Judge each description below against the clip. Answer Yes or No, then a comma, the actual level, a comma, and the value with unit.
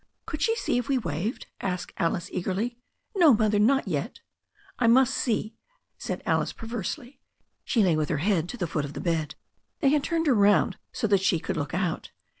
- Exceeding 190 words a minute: Yes, average, 200 wpm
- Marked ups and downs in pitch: Yes, wide, 6.2 semitones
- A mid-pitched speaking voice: No, high, 210 Hz